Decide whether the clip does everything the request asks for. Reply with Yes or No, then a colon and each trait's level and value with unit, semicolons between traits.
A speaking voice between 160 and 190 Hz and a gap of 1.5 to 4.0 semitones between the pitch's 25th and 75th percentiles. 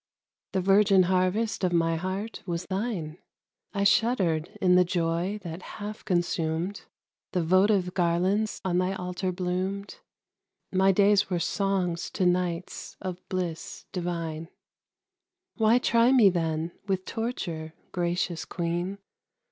Yes: medium, 185 Hz; narrow, 2.5 semitones